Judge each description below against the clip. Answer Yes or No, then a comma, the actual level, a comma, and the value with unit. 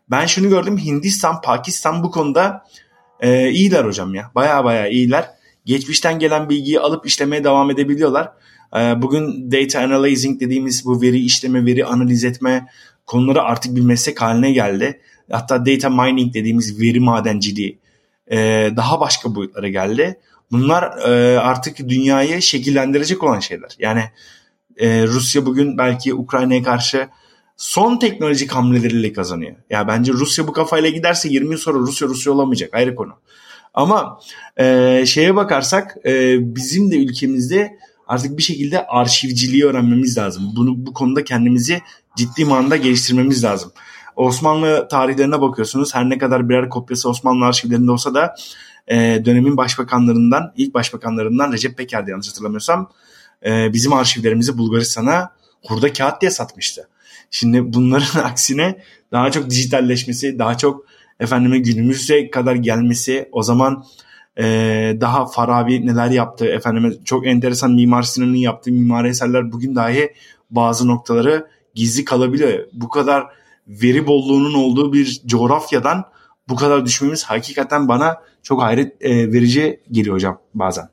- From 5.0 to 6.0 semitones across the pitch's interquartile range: No, average, 2.9 semitones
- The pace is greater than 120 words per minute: Yes, average, 135 wpm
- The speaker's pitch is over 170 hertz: No, low, 130 Hz